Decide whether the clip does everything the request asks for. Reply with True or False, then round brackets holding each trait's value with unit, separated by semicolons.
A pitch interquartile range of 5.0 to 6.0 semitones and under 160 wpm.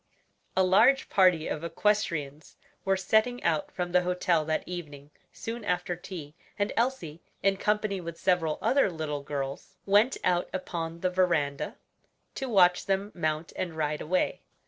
False (3.7 semitones; 150 wpm)